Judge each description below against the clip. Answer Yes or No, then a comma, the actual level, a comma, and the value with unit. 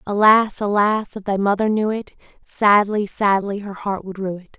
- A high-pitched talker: Yes, high, 205 Hz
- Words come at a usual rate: Yes, average, 185 wpm